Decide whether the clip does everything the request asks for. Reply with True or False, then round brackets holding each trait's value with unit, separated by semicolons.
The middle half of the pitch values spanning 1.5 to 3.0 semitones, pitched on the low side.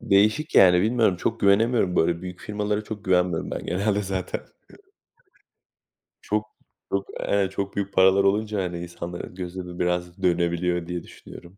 True (2.6 semitones; 95 Hz)